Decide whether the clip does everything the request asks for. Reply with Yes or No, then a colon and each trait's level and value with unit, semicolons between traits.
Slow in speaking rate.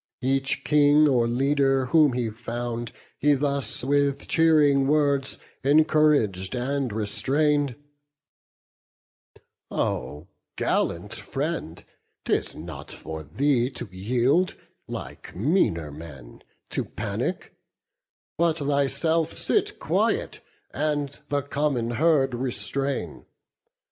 Yes: slow, 95 wpm